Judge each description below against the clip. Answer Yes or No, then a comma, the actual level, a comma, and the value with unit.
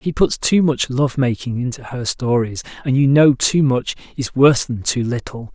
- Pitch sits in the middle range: No, low, 130 Hz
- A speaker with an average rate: Yes, average, 195 wpm